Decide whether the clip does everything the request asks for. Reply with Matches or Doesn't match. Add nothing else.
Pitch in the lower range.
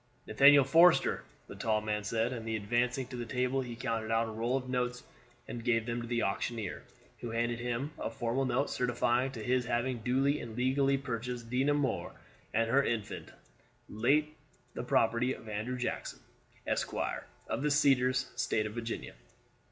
Matches